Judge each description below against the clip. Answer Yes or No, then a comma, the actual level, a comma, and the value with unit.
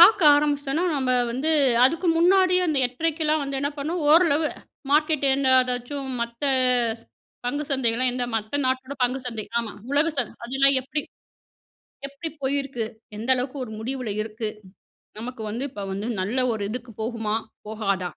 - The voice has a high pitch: Yes, very high, 265 Hz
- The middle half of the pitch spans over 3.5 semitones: Yes, average, 3.9 semitones